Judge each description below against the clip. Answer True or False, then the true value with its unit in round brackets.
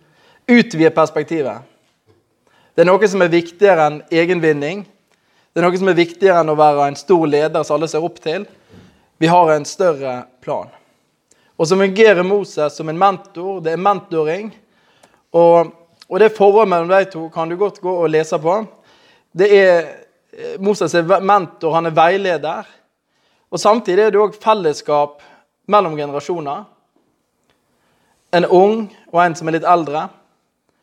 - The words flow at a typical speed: True (155 wpm)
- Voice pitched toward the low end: False (175 Hz)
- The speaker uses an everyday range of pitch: True (3.7 semitones)